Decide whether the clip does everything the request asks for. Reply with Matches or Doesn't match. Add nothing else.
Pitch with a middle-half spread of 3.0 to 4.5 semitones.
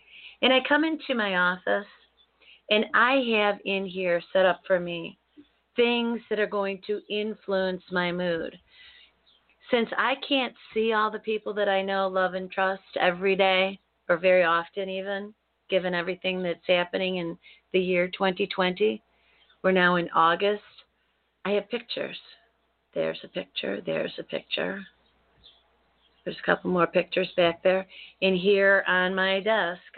Doesn't match